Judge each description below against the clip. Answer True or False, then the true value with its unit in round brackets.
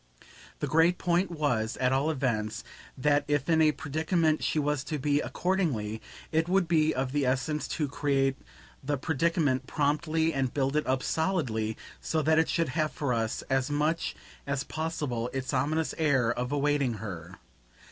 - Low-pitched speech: False (145 Hz)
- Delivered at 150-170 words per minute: True (165 wpm)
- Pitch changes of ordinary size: True (3.5 semitones)